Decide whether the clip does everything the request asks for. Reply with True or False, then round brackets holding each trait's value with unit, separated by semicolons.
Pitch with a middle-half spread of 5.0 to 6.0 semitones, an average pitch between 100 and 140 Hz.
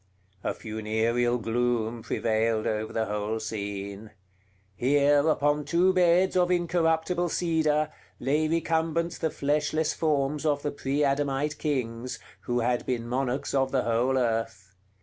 True (5.3 semitones; 135 Hz)